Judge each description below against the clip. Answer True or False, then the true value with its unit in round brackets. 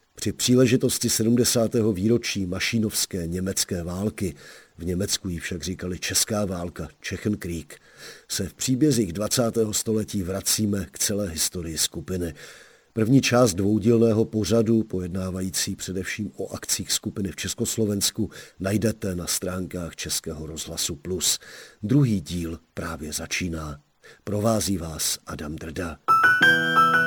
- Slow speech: True (110 wpm)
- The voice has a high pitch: False (100 Hz)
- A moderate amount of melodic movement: True (4.3 semitones)